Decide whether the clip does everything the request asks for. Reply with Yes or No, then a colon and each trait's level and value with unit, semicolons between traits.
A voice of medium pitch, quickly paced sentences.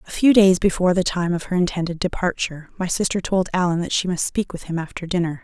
Yes: medium, 180 Hz; fast, 245 wpm